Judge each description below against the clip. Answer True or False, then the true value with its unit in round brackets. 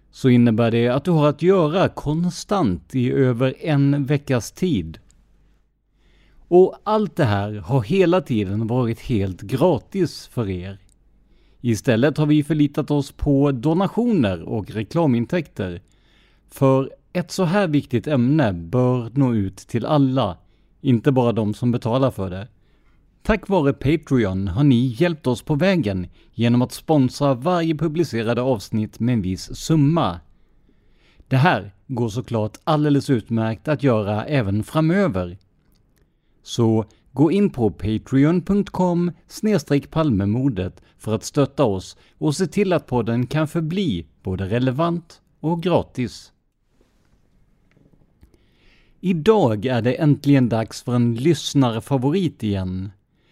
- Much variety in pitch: True (6.1 semitones)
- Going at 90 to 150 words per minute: True (125 wpm)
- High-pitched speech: False (130 Hz)